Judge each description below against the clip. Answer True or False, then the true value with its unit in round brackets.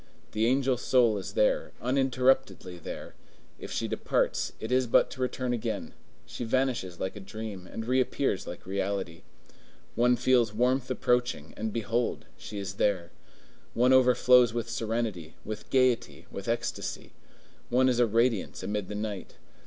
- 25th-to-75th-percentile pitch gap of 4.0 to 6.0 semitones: False (3.6 semitones)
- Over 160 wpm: False (150 wpm)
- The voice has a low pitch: True (115 Hz)